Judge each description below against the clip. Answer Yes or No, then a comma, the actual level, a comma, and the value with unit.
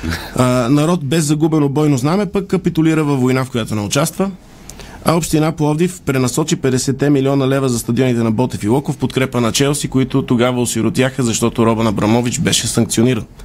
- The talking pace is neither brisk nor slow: No, fast, 170 wpm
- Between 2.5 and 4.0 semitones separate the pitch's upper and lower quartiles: No, average, 4.5 semitones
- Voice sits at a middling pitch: No, low, 130 Hz